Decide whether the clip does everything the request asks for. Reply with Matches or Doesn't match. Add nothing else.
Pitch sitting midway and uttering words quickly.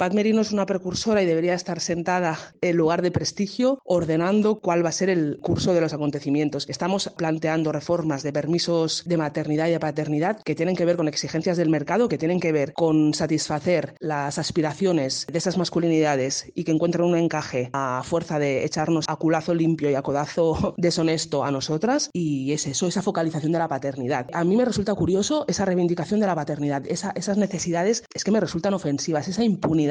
Matches